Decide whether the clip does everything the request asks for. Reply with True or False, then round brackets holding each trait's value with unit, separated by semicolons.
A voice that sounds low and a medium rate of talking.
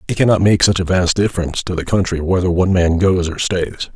False (90 Hz; 240 wpm)